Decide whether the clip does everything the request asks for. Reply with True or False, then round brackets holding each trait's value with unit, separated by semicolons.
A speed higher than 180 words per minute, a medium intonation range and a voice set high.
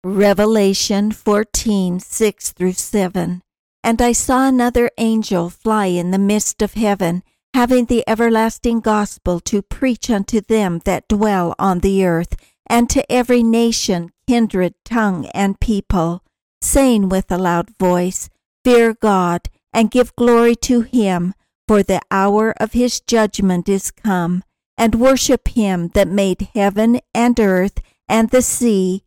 False (140 wpm; 3.6 semitones; 210 Hz)